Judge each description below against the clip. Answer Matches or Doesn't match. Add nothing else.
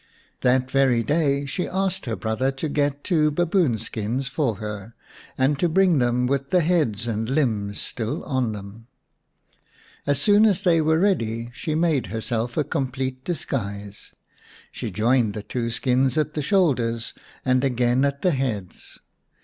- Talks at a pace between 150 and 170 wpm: Matches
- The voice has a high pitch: Doesn't match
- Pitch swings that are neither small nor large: Matches